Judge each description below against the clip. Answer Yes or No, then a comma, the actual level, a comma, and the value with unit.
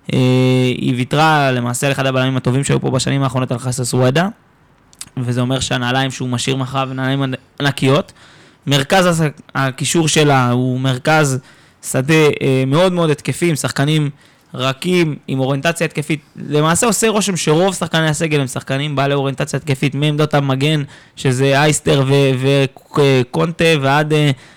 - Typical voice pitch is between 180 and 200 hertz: No, medium, 140 Hz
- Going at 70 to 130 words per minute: No, average, 145 wpm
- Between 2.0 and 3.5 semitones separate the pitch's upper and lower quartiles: Yes, average, 2.8 semitones